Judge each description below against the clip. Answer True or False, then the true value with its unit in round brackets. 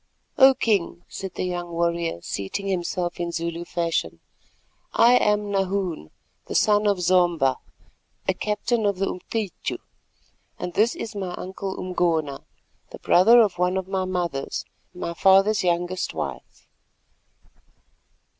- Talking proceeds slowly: True (125 wpm)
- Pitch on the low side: False (185 Hz)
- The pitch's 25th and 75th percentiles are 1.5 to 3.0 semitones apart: True (2.7 semitones)